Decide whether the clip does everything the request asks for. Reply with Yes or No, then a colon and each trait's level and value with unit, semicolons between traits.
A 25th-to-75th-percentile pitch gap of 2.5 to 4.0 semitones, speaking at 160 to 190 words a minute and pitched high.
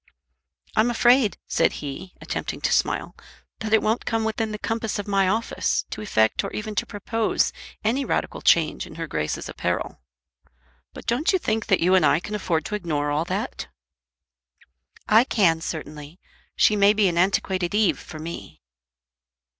No: average, 4.9 semitones; average, 170 wpm; high, 200 Hz